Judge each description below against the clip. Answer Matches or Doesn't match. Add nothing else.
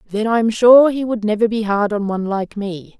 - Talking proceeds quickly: Matches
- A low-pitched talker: Doesn't match